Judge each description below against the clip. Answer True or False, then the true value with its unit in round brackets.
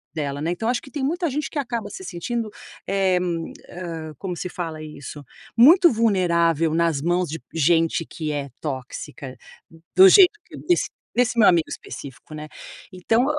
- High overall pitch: False (175 Hz)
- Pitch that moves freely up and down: True (6.9 semitones)